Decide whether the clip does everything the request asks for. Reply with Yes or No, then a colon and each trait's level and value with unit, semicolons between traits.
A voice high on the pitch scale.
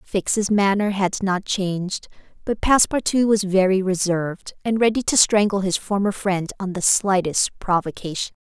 Yes: high, 195 Hz